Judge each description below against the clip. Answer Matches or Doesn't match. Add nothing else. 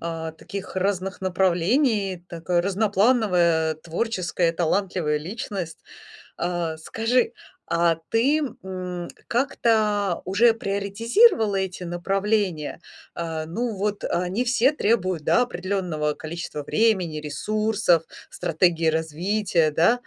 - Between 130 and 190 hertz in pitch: Matches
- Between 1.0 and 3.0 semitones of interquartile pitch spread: Doesn't match